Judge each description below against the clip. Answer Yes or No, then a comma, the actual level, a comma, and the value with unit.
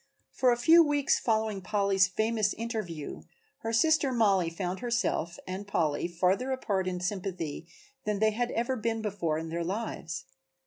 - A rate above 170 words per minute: No, average, 155 wpm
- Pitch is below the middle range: No, high, 205 Hz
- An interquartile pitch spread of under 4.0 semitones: No, average, 4.5 semitones